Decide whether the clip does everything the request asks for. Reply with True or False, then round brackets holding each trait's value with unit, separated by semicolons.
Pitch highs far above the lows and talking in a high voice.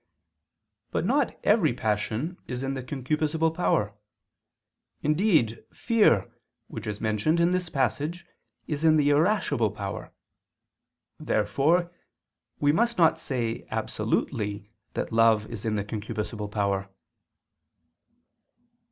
False (7.1 semitones; 130 Hz)